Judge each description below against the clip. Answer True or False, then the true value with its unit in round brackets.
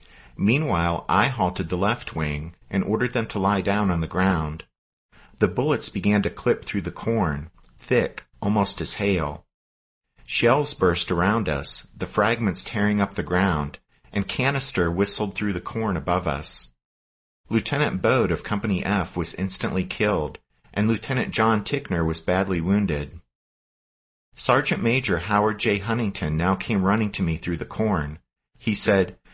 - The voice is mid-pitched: False (95 Hz)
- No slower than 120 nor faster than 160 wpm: True (155 wpm)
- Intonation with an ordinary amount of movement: True (4.4 semitones)